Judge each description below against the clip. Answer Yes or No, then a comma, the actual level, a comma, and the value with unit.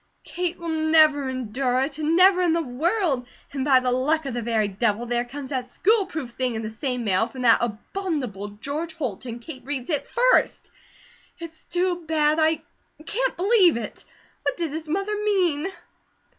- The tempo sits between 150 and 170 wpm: No, average, 180 wpm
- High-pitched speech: Yes, very high, 290 Hz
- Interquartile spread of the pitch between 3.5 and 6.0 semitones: Yes, wide, 5.5 semitones